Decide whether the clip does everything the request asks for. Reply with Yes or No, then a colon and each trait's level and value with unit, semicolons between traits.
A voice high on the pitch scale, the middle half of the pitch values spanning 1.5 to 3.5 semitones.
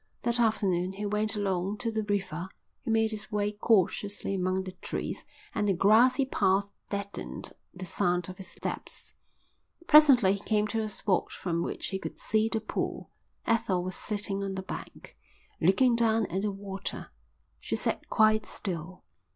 Yes: high, 205 Hz; narrow, 2.5 semitones